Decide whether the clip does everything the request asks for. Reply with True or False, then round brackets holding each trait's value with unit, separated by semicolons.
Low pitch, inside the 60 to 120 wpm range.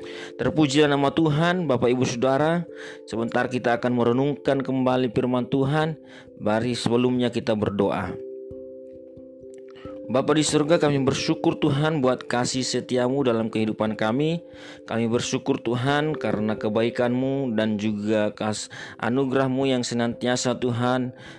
True (125 Hz; 115 wpm)